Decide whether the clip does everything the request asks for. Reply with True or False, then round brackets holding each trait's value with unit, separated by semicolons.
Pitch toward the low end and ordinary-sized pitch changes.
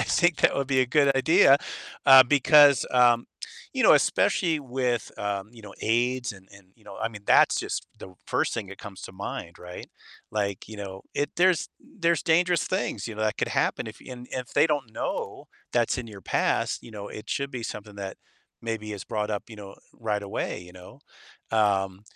True (115 Hz; 4.9 semitones)